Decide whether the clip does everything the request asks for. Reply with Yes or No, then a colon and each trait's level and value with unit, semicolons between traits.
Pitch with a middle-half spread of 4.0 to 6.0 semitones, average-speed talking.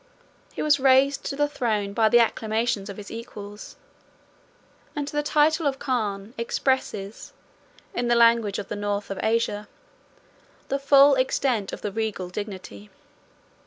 Yes: average, 4.6 semitones; average, 145 wpm